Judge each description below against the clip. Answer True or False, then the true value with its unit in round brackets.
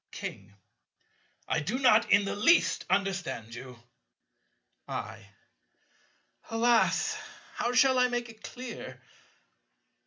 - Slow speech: True (100 wpm)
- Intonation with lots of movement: True (7.4 semitones)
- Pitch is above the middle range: True (220 Hz)